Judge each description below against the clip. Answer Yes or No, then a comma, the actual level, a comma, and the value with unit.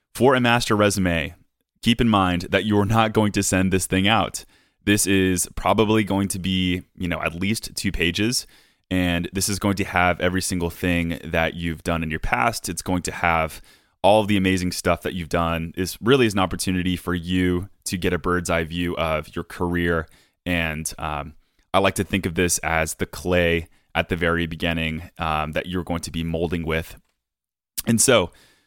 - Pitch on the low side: Yes, very low, 90 Hz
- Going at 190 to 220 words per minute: Yes, average, 200 wpm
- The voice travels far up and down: No, narrow, 2.5 semitones